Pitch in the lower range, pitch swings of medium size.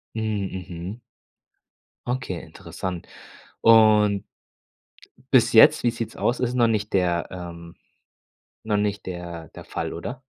Yes: low, 100 Hz; average, 4.5 semitones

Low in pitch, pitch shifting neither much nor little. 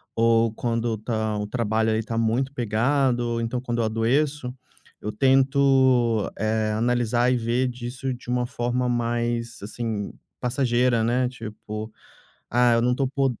No: low, 120 Hz; narrow, 1.9 semitones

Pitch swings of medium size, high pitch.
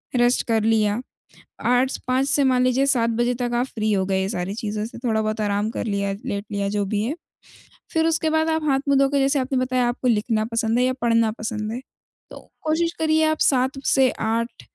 Yes: average, 3.8 semitones; high, 240 Hz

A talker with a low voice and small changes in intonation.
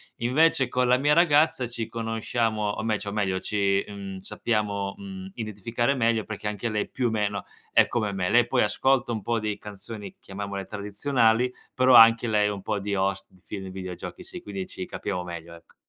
No: low, 105 Hz; average, 3.1 semitones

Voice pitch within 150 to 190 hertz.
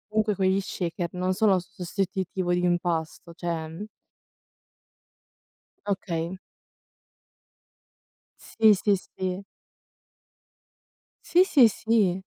Yes: medium, 185 Hz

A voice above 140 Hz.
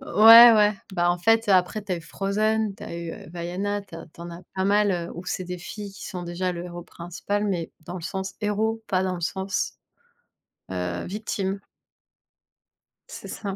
Yes: high, 190 Hz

